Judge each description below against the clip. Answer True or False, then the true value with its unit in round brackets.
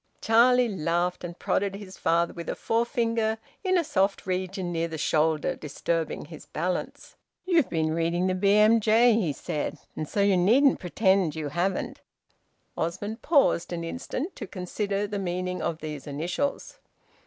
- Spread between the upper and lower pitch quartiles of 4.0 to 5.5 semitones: True (4.7 semitones)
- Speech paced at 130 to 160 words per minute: True (155 wpm)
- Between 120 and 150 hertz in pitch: False (185 Hz)